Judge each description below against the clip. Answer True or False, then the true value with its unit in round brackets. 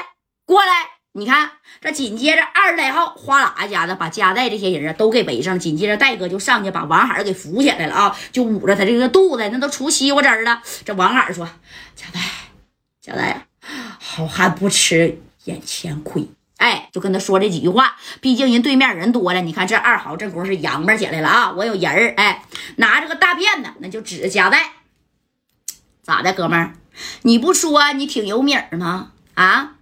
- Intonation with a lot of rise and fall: True (6.9 semitones)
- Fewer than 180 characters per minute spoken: False (280 characters per minute)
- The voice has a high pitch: True (215 Hz)